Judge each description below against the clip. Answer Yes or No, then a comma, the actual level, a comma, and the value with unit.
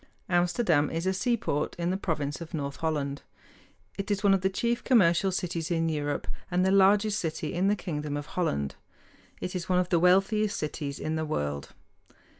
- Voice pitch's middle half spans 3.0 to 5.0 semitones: Yes, average, 4.1 semitones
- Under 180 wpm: No, average, 190 wpm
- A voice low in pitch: No, medium, 175 Hz